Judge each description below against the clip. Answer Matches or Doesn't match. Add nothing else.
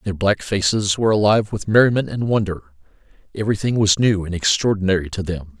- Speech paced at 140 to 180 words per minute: Matches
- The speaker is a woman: Doesn't match